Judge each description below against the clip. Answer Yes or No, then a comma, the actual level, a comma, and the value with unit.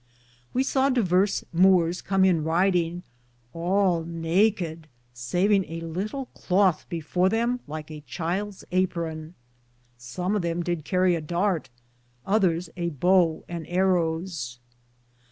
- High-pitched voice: No, medium, 175 Hz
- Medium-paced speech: No, slow, 120 wpm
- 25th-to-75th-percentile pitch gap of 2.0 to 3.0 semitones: Yes, average, 2.7 semitones